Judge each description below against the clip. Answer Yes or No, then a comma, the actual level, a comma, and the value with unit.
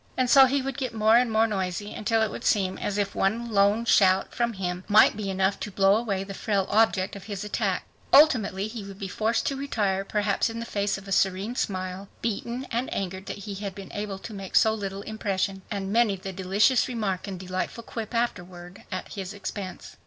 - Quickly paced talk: Yes, fast, 215 wpm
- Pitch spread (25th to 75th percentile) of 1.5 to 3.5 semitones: Yes, narrow, 2.6 semitones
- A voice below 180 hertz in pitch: No, high, 205 Hz